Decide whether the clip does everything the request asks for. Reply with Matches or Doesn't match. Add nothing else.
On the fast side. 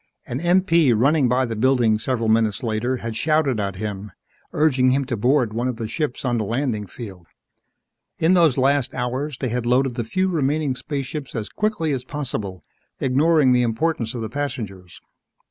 Doesn't match